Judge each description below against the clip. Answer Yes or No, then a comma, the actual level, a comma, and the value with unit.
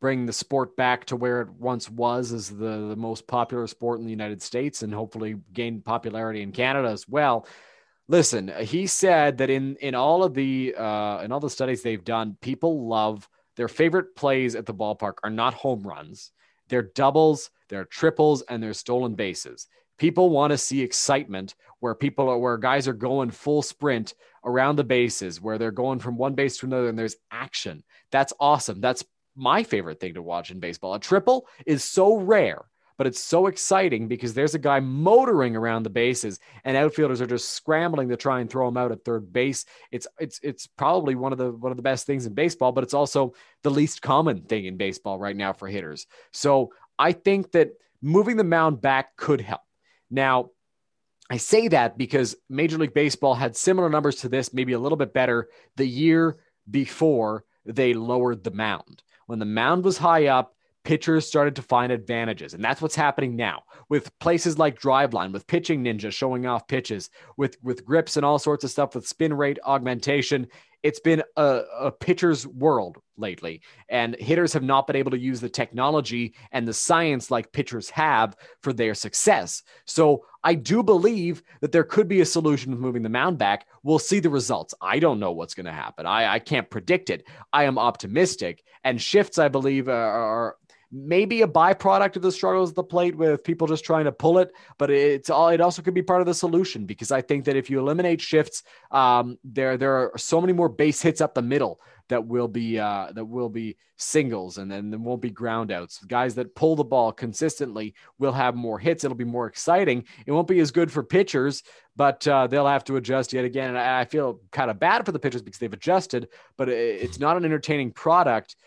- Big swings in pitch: No, average, 4.7 semitones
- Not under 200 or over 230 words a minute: Yes, fast, 205 wpm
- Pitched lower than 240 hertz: Yes, low, 135 Hz